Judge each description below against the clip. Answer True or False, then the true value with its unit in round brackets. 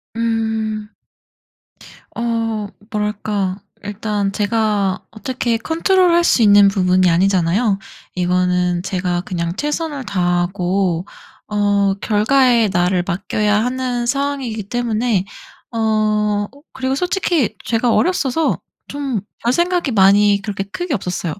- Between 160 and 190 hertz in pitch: False (210 Hz)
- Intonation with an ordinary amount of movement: True (4.1 semitones)